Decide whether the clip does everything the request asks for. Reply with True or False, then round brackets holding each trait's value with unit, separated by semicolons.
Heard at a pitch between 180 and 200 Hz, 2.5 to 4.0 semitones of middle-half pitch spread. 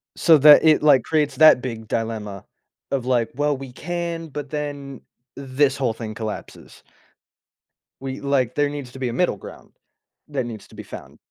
False (135 Hz; 3.7 semitones)